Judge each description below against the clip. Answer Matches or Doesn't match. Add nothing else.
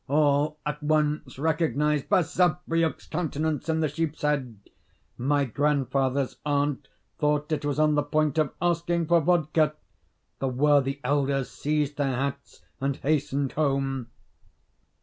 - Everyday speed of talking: Doesn't match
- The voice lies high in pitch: Doesn't match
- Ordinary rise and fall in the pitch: Doesn't match